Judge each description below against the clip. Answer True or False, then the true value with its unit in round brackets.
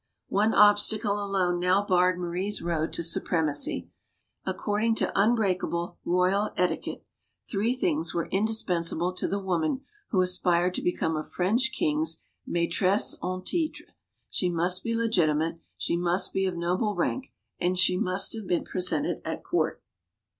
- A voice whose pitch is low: False (185 Hz)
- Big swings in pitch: False (3.0 semitones)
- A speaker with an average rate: True (145 wpm)